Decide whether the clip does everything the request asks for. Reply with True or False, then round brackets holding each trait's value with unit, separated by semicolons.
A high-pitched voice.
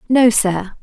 True (220 Hz)